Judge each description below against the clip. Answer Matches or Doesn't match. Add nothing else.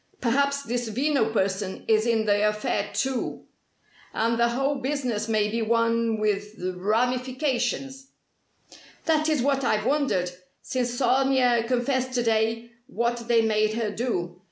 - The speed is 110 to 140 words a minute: Matches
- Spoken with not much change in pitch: Doesn't match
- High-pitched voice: Matches